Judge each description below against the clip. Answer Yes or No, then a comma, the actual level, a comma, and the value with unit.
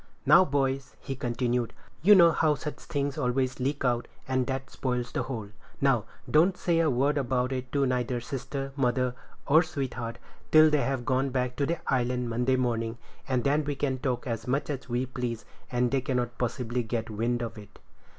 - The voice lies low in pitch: Yes, low, 130 Hz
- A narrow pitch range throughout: Yes, narrow, 2.3 semitones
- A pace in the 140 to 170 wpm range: No, average, 190 wpm